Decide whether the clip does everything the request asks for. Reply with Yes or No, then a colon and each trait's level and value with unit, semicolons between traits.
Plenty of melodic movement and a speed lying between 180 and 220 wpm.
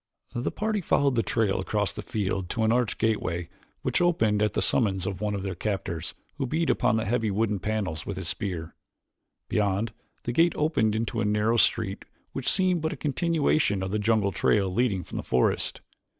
No: average, 4.0 semitones; average, 195 wpm